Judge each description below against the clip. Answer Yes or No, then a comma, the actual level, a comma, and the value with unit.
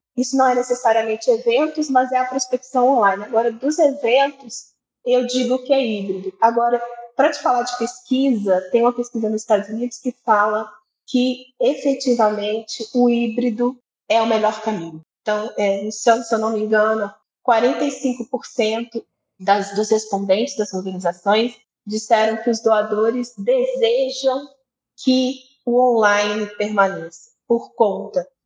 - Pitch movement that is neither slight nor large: Yes, average, 3.1 semitones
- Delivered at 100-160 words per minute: Yes, average, 140 wpm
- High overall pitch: Yes, high, 235 Hz